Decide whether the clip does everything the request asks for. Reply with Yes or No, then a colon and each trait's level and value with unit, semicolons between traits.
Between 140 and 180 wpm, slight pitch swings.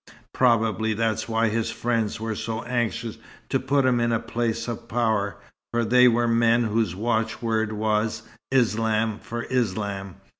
Yes: average, 150 wpm; narrow, 1.4 semitones